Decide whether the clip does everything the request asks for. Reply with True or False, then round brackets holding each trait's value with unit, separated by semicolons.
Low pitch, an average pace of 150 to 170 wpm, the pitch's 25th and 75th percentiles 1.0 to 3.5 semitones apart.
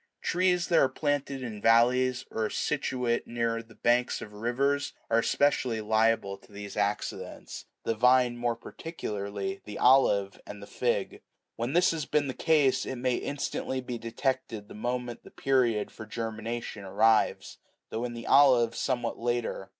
True (120 Hz; 160 wpm; 2.9 semitones)